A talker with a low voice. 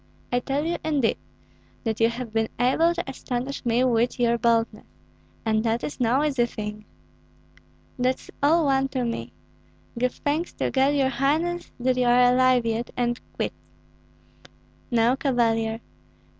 No: high, 245 Hz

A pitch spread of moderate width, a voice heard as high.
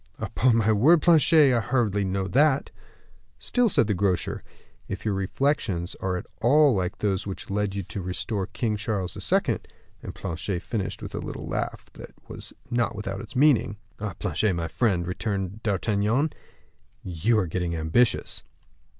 No: average, 4.1 semitones; low, 105 Hz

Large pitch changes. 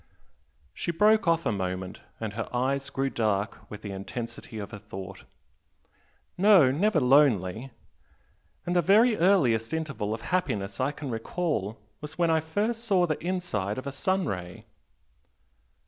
Yes: wide, 8.8 semitones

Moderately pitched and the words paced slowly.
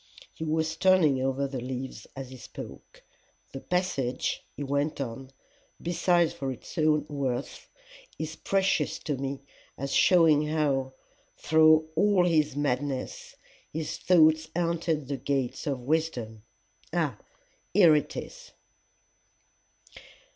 Yes: medium, 150 Hz; slow, 120 wpm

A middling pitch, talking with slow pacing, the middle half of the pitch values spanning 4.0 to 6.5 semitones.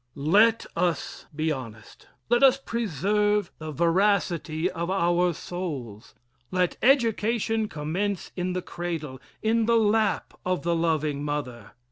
Yes: medium, 175 Hz; slow, 125 wpm; average, 5.2 semitones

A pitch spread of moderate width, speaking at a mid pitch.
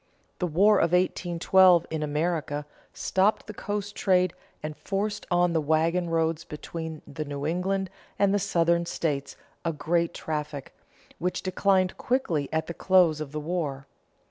Yes: average, 3.3 semitones; medium, 170 Hz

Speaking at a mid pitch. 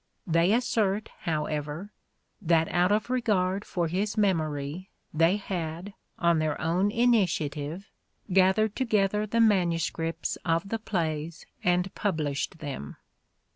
Yes: medium, 180 Hz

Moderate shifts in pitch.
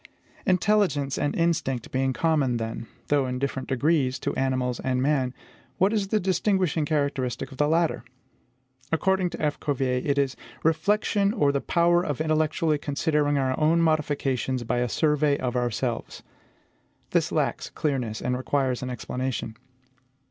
Yes: average, 4.0 semitones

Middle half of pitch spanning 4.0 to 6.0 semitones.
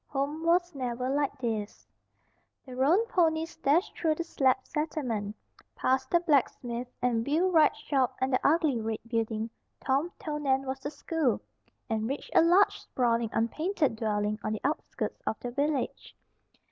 Yes: average, 5.1 semitones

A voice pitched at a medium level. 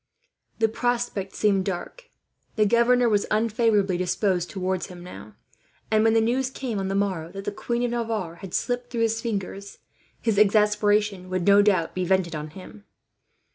No: high, 205 Hz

